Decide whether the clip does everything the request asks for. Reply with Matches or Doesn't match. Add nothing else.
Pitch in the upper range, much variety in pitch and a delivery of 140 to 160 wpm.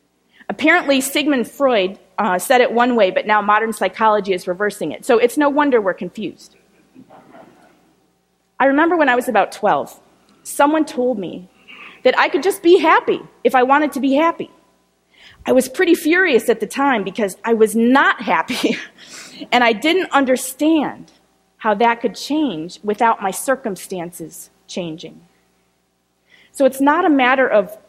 Matches